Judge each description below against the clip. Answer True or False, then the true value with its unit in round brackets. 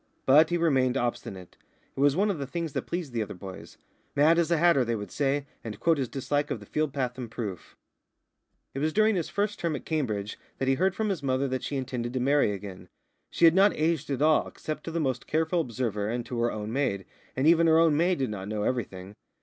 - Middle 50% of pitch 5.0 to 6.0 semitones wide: True (5.6 semitones)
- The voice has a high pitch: False (135 Hz)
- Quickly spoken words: True (240 wpm)